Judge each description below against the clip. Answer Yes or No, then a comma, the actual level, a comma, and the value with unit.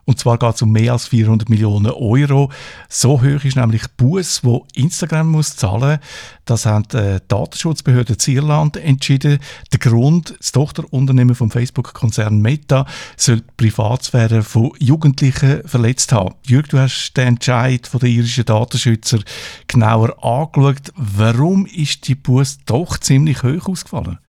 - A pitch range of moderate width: Yes, average, 3.3 semitones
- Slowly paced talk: No, average, 150 wpm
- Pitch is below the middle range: Yes, low, 130 Hz